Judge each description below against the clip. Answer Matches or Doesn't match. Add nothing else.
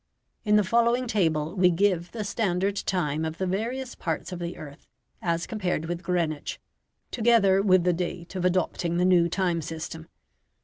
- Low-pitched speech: Doesn't match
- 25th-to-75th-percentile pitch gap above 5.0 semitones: Doesn't match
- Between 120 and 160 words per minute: Doesn't match